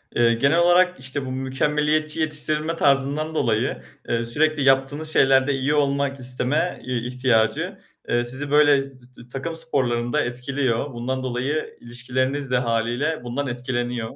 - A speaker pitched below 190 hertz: Yes, low, 135 Hz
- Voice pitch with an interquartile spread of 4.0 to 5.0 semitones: No, average, 3.3 semitones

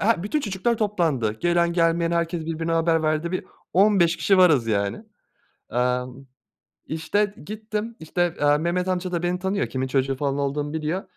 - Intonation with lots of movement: No, average, 4.2 semitones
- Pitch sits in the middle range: Yes, medium, 170 Hz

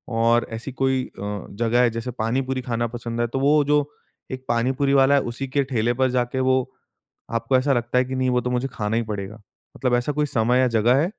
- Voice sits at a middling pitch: No, low, 125 Hz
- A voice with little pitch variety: Yes, narrow, 2.2 semitones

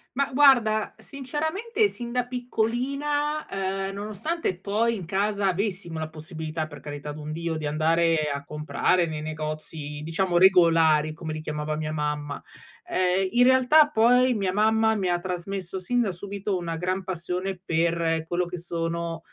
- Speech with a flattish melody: No, wide, 5.6 semitones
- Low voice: No, medium, 180 Hz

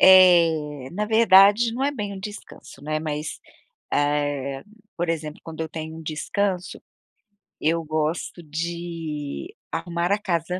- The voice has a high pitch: No, medium, 165 Hz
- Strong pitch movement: No, average, 3.6 semitones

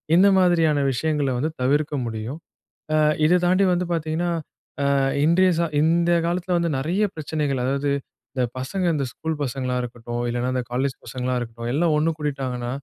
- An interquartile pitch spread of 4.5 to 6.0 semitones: Yes, average, 4.9 semitones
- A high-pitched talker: No, medium, 150 Hz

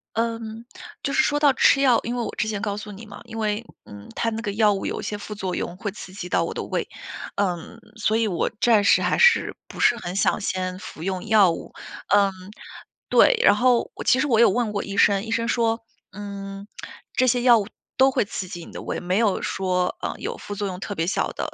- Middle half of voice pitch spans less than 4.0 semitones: Yes, average, 2.9 semitones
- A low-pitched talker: No, high, 210 Hz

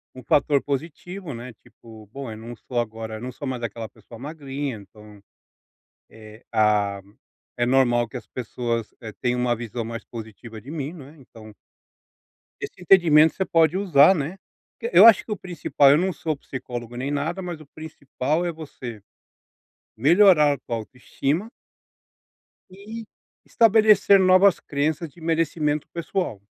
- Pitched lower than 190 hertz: Yes, medium, 140 Hz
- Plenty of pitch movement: Yes, wide, 6.1 semitones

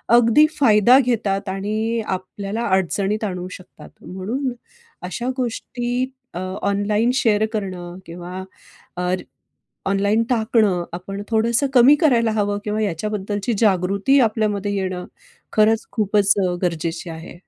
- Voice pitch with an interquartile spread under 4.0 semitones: Yes, average, 3.4 semitones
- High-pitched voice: Yes, high, 205 Hz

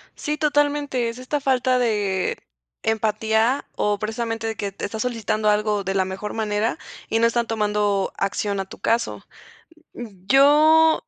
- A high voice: Yes, high, 225 Hz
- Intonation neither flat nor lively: Yes, average, 3.4 semitones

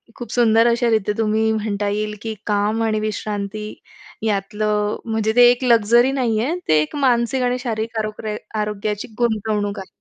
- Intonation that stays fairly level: Yes, narrow, 1.9 semitones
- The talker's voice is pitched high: Yes, high, 220 Hz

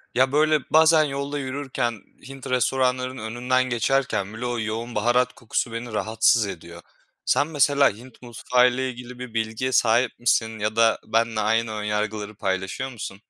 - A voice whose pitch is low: Yes, low, 120 Hz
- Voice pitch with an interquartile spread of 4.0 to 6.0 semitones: No, average, 2.8 semitones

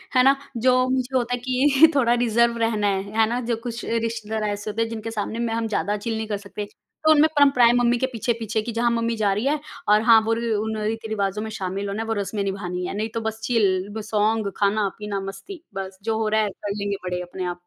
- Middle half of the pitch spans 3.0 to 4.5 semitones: No, narrow, 2.5 semitones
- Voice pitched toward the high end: Yes, high, 220 Hz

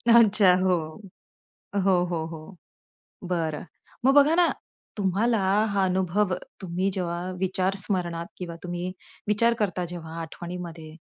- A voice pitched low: No, medium, 185 Hz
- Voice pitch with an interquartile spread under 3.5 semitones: Yes, average, 2.7 semitones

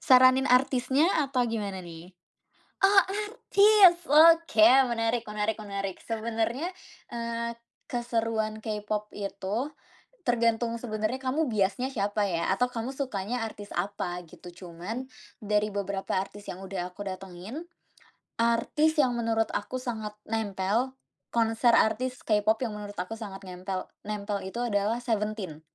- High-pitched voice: Yes, high, 225 Hz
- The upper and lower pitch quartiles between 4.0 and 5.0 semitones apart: No, average, 3.4 semitones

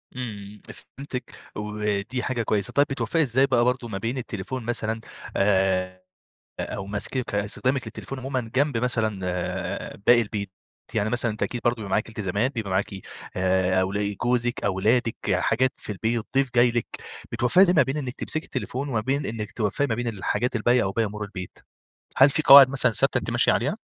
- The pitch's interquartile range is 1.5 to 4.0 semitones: Yes, average, 3.7 semitones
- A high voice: No, low, 115 Hz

